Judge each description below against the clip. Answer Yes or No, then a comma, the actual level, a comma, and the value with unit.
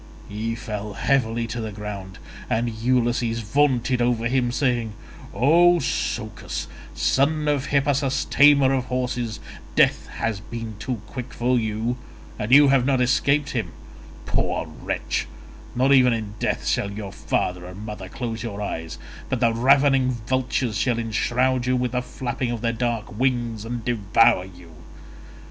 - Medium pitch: No, low, 120 Hz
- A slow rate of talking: No, average, 150 wpm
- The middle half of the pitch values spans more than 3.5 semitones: No, average, 3.0 semitones